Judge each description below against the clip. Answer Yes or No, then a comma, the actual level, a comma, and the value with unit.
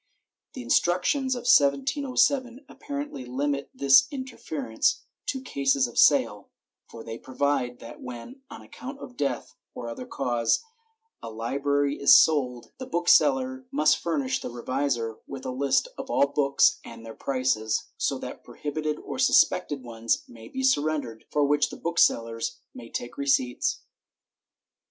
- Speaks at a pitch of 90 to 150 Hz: Yes, medium, 140 Hz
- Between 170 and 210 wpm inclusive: No, average, 145 wpm